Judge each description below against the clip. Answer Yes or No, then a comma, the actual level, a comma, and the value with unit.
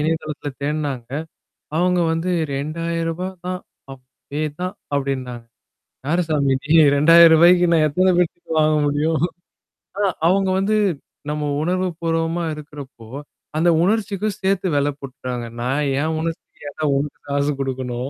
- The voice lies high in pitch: No, medium, 155 Hz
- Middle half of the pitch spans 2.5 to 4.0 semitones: Yes, average, 3.7 semitones